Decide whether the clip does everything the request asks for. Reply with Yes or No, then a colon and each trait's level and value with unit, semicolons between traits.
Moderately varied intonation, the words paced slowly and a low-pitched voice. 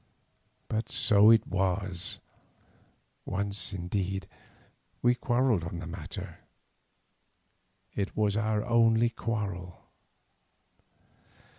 Yes: average, 3.4 semitones; slow, 85 wpm; low, 100 Hz